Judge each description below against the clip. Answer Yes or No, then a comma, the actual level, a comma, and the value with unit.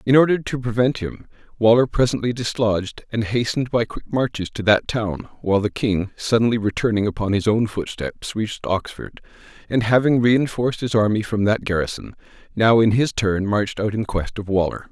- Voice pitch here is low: Yes, low, 110 Hz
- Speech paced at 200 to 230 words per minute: No, average, 180 wpm